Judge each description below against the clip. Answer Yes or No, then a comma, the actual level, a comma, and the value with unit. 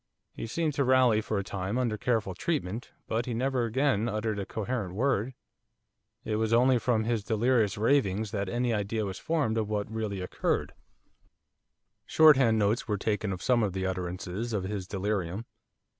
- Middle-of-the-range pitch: No, low, 110 Hz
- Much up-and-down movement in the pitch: No, average, 3.4 semitones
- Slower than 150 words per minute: No, average, 175 wpm